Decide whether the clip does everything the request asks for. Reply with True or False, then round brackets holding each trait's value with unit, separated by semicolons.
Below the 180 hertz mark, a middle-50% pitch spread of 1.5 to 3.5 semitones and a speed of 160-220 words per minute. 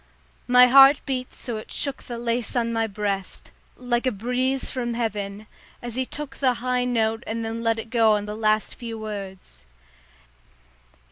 False (230 Hz; 2.5 semitones; 175 wpm)